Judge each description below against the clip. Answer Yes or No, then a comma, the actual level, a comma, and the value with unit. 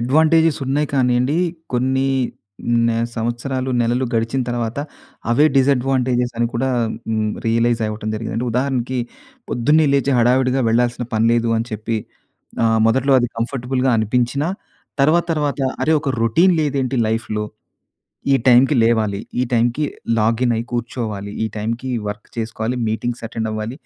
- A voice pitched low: Yes, low, 120 Hz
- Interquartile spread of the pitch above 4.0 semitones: No, average, 2.8 semitones